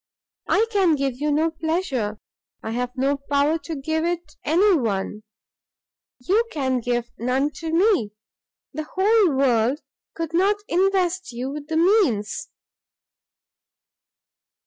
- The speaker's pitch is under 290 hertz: No, very high, 300 Hz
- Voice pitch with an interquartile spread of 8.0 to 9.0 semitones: No, wide, 5.6 semitones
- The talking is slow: Yes, slow, 125 wpm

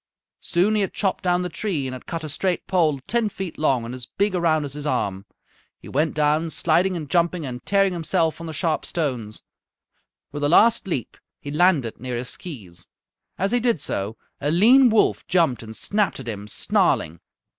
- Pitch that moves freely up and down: Yes, wide, 6.2 semitones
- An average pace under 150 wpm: No, average, 200 wpm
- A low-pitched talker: No, medium, 160 Hz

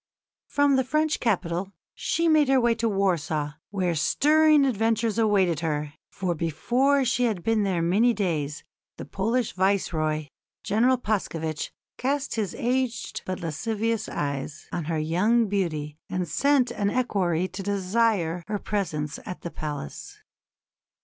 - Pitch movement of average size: No, wide, 6.1 semitones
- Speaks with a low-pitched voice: No, high, 200 Hz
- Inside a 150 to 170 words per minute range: No, average, 140 wpm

